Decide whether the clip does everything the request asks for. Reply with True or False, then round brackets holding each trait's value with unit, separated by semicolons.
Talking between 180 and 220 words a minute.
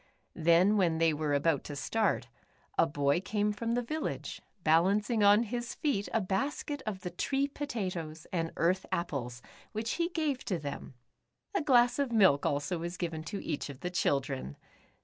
False (170 wpm)